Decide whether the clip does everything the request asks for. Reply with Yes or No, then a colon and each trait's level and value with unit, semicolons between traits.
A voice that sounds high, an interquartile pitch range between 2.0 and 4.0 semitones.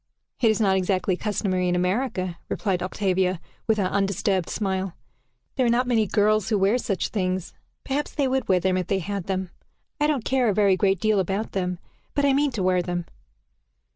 Yes: high, 195 Hz; average, 3.0 semitones